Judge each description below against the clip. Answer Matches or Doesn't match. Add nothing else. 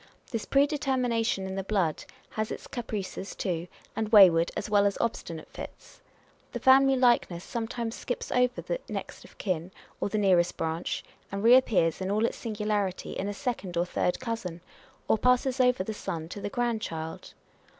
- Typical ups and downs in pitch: Matches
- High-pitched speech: Matches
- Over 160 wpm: Matches